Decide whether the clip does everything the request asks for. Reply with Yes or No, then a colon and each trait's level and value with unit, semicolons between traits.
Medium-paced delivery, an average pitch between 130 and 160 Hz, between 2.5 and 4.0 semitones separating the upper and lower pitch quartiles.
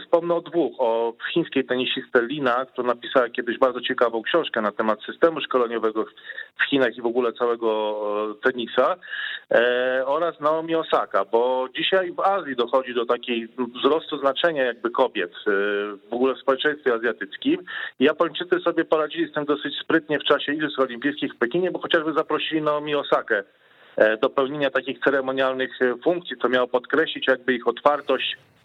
No: average, 150 wpm; low, 135 Hz; average, 4.5 semitones